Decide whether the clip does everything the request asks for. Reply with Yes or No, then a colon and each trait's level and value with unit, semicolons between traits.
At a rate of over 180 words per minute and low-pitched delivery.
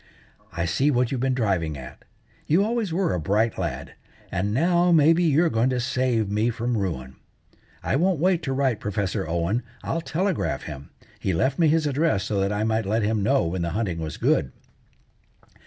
Yes: average, 190 wpm; low, 115 Hz